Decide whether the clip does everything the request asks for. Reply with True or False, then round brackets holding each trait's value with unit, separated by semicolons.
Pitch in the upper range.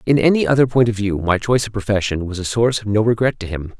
False (110 Hz)